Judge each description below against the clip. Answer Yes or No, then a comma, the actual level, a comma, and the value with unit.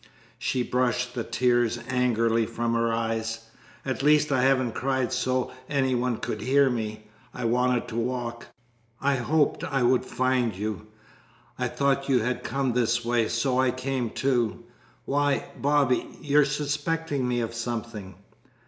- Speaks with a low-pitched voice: Yes, low, 125 Hz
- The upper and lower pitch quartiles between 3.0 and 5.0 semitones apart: No, narrow, 2.6 semitones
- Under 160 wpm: Yes, average, 150 wpm